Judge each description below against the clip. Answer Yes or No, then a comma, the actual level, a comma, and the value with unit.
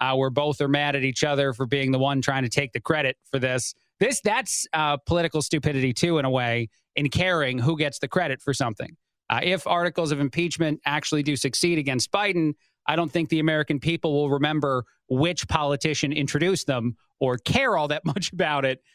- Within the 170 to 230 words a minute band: Yes, fast, 205 wpm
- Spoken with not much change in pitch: No, average, 3.1 semitones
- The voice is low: No, medium, 145 Hz